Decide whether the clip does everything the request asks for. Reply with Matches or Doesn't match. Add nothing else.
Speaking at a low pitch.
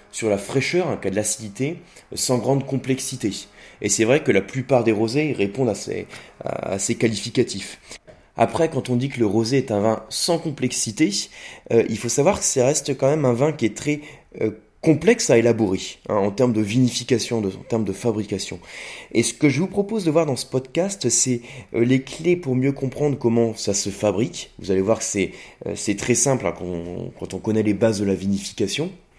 Matches